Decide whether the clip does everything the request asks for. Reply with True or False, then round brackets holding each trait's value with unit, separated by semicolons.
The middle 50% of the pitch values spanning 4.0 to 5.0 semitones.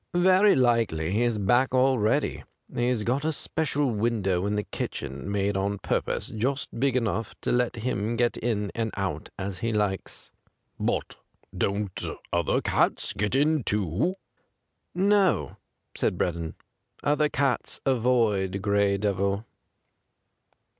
True (4.4 semitones)